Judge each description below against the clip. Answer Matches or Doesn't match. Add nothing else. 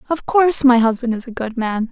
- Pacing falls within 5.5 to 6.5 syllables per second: Matches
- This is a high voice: Matches